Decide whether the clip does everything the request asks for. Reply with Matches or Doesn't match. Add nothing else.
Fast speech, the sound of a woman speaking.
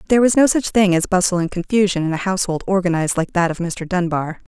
Matches